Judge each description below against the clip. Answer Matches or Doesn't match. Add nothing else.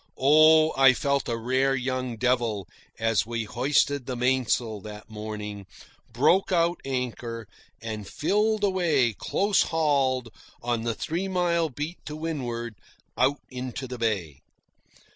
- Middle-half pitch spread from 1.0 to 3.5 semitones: Doesn't match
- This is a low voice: Matches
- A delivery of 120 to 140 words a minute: Matches